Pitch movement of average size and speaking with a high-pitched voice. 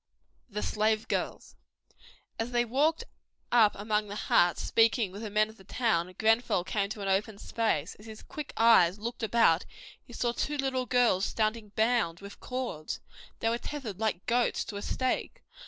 Yes: average, 3.0 semitones; high, 220 Hz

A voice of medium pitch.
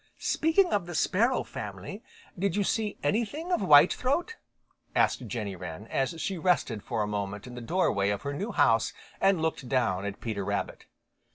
Yes: medium, 150 Hz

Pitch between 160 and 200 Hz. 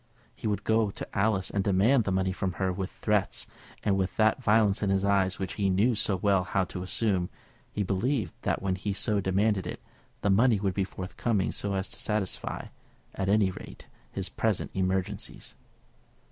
No: low, 100 Hz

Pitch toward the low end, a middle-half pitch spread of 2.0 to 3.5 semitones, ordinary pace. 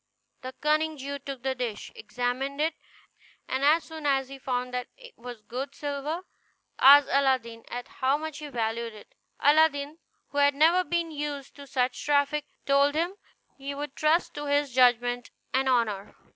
No: very high, 280 Hz; average, 2.9 semitones; average, 170 wpm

